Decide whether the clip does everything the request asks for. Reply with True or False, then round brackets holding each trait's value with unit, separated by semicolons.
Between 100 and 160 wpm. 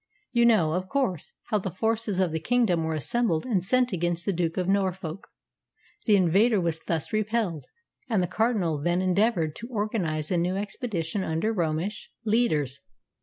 False (170 wpm)